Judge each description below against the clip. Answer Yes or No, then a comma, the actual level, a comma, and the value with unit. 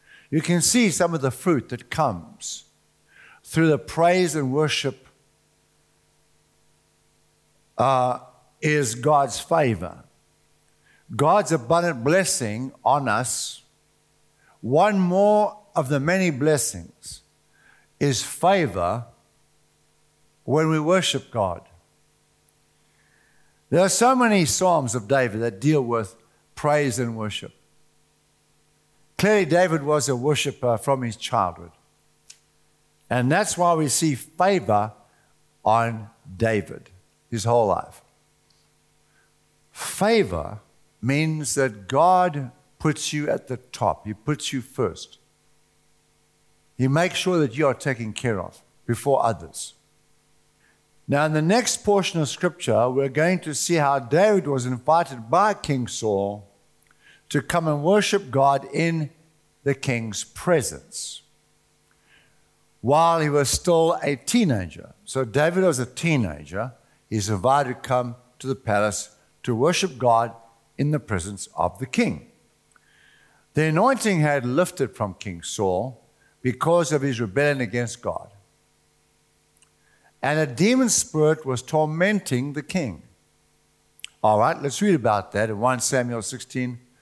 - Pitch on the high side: No, medium, 140 Hz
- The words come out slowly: Yes, slow, 120 wpm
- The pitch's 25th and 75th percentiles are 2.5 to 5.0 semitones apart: No, wide, 5.5 semitones